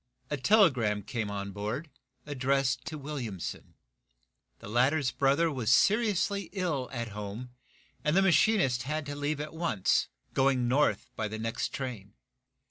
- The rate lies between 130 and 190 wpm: Yes, average, 140 wpm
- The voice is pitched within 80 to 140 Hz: Yes, low, 135 Hz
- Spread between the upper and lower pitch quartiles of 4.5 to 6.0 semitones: Yes, average, 5.2 semitones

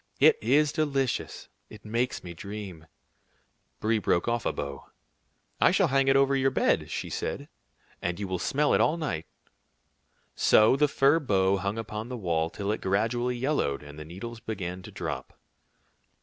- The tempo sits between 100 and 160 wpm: No, average, 170 wpm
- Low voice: Yes, low, 110 Hz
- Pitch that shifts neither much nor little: No, wide, 6.4 semitones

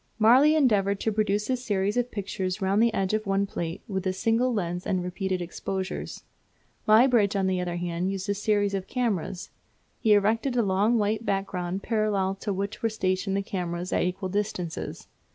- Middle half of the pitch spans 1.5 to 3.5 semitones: Yes, narrow, 2.5 semitones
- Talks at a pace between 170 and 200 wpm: Yes, average, 185 wpm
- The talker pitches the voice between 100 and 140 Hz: No, high, 200 Hz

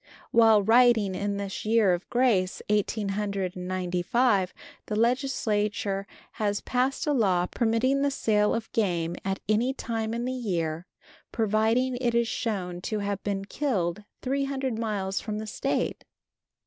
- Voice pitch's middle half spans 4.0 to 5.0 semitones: No, average, 3.5 semitones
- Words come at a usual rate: Yes, average, 150 wpm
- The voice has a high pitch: Yes, high, 215 Hz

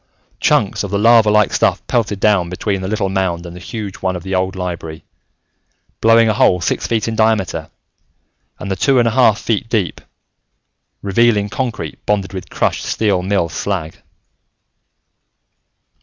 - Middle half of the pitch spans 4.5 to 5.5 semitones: No, average, 3.2 semitones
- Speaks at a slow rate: No, average, 160 wpm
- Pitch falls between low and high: No, low, 100 Hz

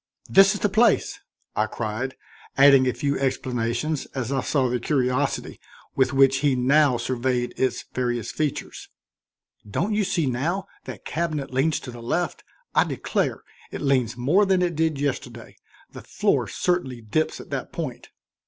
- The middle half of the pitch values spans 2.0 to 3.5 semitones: No, average, 4.1 semitones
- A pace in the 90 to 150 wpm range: No, average, 160 wpm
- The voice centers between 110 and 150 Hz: Yes, low, 135 Hz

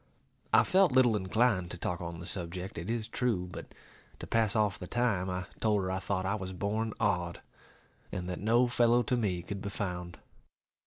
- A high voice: No, low, 100 Hz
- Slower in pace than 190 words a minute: No, average, 200 wpm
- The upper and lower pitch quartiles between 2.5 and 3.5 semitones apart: No, average, 4.0 semitones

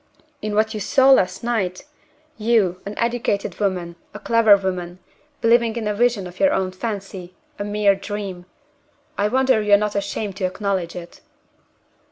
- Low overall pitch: No, high, 205 Hz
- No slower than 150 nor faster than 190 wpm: Yes, average, 165 wpm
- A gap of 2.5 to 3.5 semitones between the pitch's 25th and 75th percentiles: Yes, average, 3.2 semitones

